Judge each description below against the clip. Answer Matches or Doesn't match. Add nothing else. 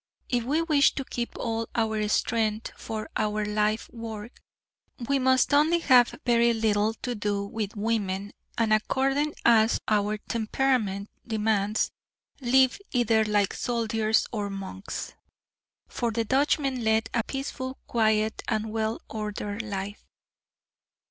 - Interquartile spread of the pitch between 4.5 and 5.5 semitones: Doesn't match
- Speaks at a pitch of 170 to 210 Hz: Doesn't match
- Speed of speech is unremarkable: Doesn't match